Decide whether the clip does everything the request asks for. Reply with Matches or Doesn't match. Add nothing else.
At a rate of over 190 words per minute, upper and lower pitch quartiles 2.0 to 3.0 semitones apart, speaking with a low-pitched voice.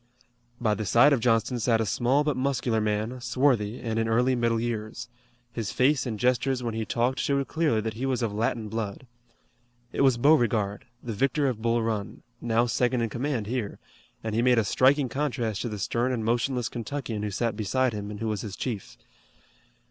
Matches